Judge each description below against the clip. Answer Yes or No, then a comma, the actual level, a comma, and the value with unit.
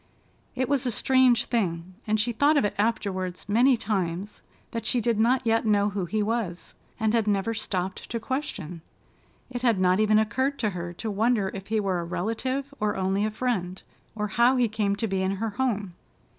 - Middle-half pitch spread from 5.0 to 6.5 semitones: No, average, 3.5 semitones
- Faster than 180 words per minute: Yes, average, 195 wpm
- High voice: Yes, high, 215 Hz